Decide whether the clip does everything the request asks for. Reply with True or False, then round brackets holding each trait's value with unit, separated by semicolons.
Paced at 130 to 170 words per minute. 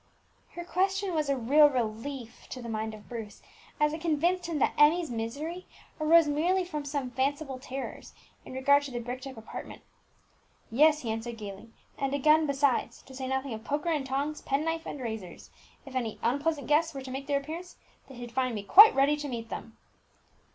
False (200 wpm)